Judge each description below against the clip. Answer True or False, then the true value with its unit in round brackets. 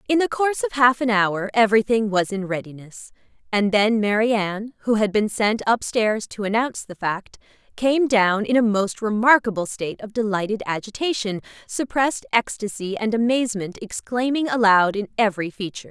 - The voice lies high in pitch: True (220 Hz)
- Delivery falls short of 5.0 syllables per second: False (5.4 syllables/s)